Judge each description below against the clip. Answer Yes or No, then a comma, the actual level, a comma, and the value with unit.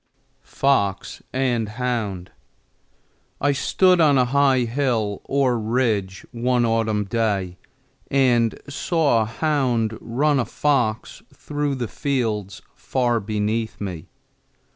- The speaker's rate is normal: No, slow, 110 wpm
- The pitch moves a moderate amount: Yes, average, 4.0 semitones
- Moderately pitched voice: No, low, 120 Hz